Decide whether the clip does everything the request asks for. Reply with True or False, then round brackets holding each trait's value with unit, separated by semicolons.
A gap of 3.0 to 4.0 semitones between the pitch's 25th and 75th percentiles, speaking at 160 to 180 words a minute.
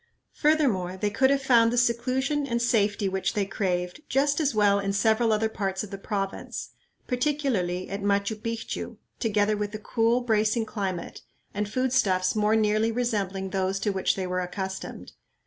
True (3.4 semitones; 170 wpm)